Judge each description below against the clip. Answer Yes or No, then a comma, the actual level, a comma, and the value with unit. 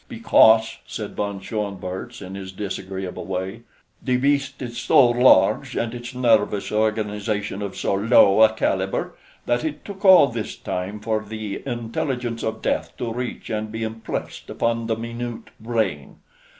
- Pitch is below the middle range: Yes, low, 110 Hz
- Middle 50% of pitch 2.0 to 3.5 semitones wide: Yes, average, 3.0 semitones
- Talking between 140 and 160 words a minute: Yes, average, 150 wpm